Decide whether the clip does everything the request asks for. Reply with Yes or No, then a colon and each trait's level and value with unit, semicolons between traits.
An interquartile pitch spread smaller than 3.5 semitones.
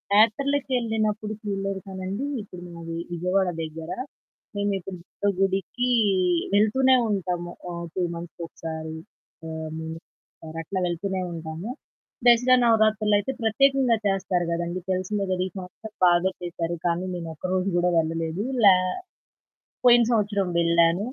No: average, 3.8 semitones